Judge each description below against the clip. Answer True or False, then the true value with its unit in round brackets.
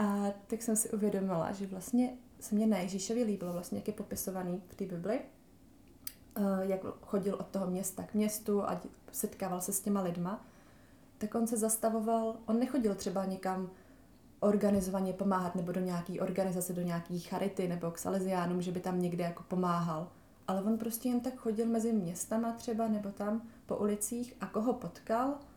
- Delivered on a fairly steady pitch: False (3.3 semitones)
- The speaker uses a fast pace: True (175 wpm)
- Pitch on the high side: True (200 Hz)